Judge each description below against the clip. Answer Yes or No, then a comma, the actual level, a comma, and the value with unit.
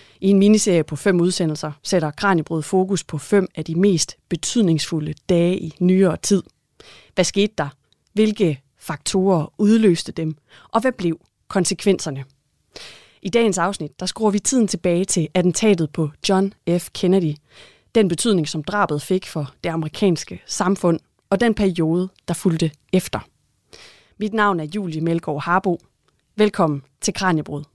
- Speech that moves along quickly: No, slow, 145 wpm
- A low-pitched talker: No, medium, 180 Hz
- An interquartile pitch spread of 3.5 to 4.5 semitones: Yes, average, 3.9 semitones